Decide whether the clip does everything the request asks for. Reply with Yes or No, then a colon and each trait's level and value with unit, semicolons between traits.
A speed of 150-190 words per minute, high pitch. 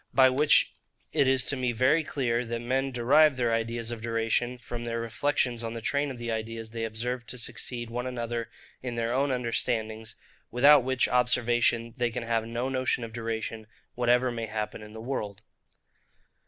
No: average, 180 wpm; low, 120 Hz